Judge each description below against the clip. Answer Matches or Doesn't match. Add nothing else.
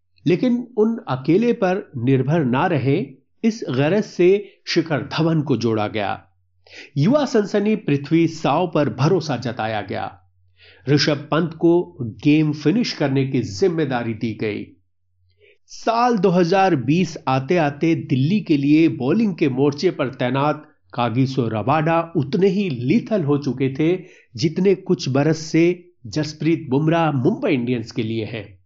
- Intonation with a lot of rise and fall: Matches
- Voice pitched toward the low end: Doesn't match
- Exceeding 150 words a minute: Doesn't match